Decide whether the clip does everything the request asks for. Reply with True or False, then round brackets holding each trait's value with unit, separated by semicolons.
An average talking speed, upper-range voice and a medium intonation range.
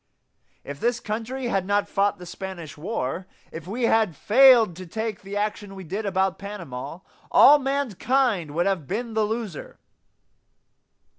True (150 wpm; 205 Hz; 4.0 semitones)